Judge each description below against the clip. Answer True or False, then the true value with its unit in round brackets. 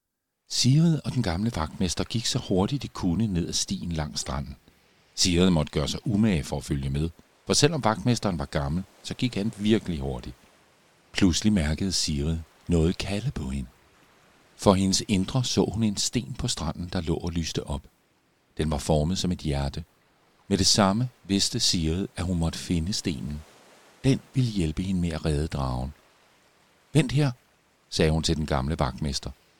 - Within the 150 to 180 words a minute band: True (175 wpm)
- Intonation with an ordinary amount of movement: False (5.7 semitones)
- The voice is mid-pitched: False (90 Hz)